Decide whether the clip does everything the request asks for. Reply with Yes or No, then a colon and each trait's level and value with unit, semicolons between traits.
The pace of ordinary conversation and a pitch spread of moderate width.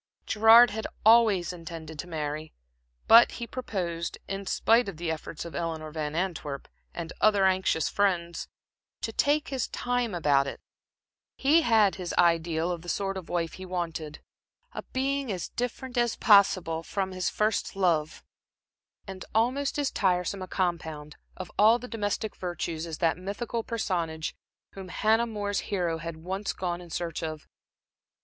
Yes: average, 155 wpm; average, 4.7 semitones